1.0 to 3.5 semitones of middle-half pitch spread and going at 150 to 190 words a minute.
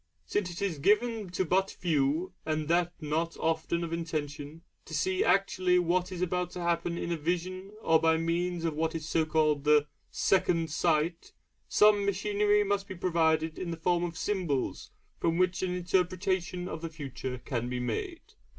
Yes: narrow, 2.6 semitones; average, 175 wpm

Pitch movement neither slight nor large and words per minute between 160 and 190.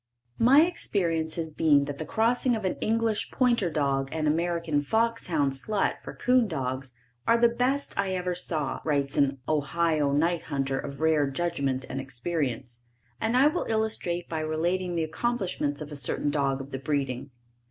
No: wide, 6.1 semitones; average, 175 wpm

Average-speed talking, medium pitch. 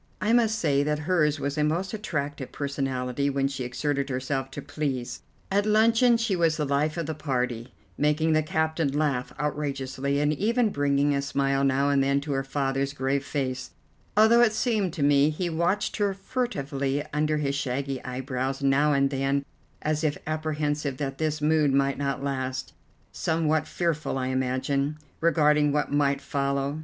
Yes: average, 170 wpm; medium, 145 Hz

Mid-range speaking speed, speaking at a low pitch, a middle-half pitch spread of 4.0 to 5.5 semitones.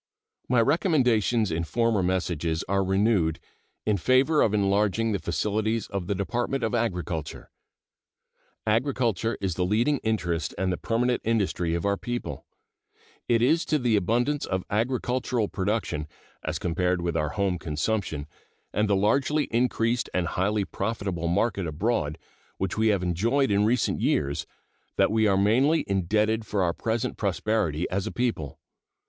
Yes: average, 150 wpm; low, 105 Hz; average, 4.3 semitones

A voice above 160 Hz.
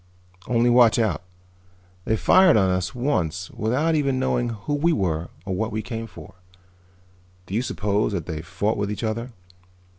No: low, 110 Hz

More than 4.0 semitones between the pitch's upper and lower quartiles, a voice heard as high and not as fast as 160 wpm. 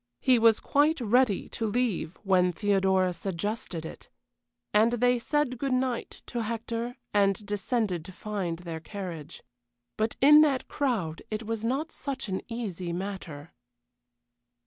Yes: average, 4.7 semitones; high, 215 Hz; average, 140 wpm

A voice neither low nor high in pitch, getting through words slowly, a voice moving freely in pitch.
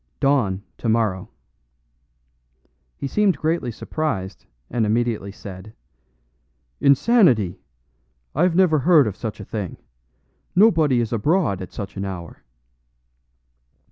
No: low, 115 Hz; slow, 105 wpm; wide, 7.8 semitones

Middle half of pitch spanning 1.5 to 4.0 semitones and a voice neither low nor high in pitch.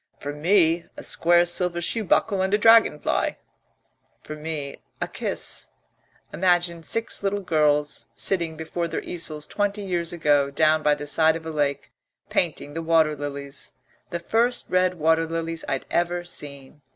Yes: average, 2.9 semitones; medium, 165 Hz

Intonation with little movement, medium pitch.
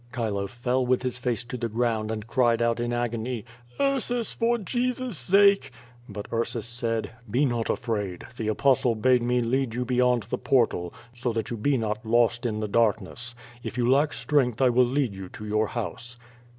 No: narrow, 2.3 semitones; low, 120 Hz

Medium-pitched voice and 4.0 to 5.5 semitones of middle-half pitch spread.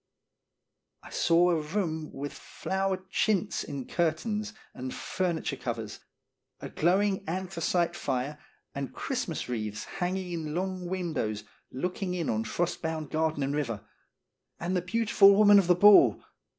Yes: medium, 170 Hz; average, 4.4 semitones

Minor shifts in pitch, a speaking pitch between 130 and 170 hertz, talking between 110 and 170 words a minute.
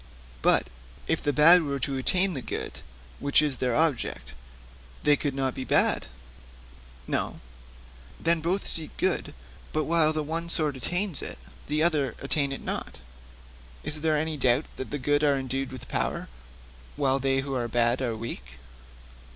No: average, 3.1 semitones; medium, 140 Hz; average, 165 wpm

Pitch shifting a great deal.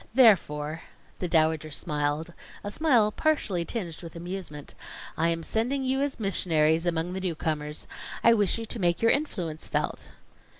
Yes: wide, 5.9 semitones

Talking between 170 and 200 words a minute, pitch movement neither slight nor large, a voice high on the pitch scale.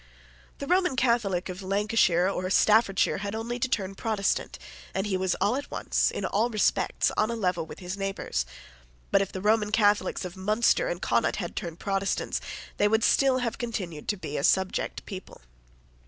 Yes: average, 180 wpm; average, 3.2 semitones; high, 200 Hz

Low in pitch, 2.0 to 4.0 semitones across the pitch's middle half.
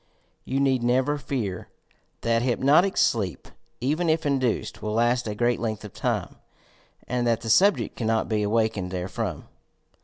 Yes: low, 120 Hz; average, 3.6 semitones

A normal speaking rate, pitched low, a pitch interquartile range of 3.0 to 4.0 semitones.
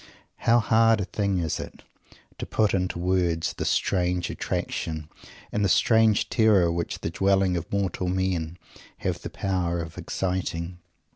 No: average, 150 wpm; very low, 90 Hz; narrow, 2.6 semitones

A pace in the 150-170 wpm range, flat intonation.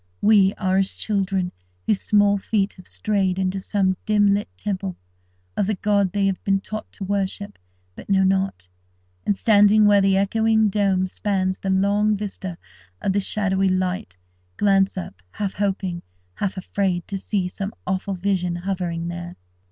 Yes: average, 160 wpm; narrow, 1.5 semitones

